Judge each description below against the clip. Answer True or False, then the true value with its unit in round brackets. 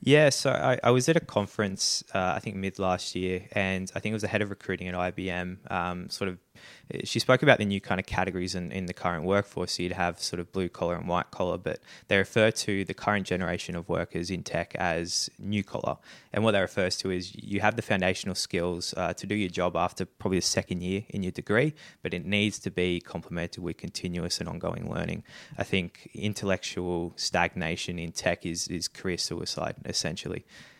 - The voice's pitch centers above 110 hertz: False (95 Hz)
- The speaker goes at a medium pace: False (215 wpm)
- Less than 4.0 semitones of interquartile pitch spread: True (2.6 semitones)